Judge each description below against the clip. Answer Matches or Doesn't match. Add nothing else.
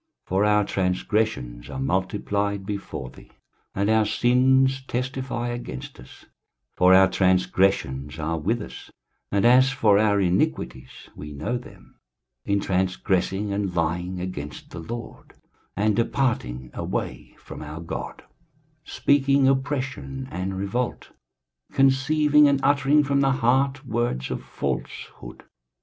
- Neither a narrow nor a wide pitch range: Doesn't match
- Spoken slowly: Matches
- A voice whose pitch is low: Matches